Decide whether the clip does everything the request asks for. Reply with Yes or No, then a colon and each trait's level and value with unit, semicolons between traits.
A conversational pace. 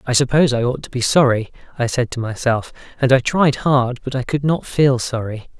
No: fast, 225 wpm